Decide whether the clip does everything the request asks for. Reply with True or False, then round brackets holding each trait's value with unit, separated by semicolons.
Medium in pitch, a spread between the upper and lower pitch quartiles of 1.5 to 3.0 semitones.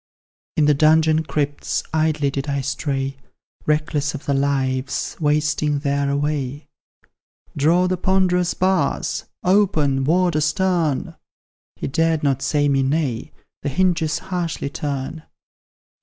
True (150 Hz; 2.5 semitones)